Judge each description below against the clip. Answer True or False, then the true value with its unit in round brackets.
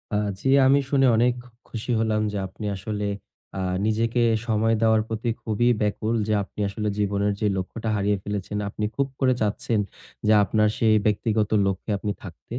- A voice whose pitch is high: False (110 Hz)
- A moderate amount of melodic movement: False (1.7 semitones)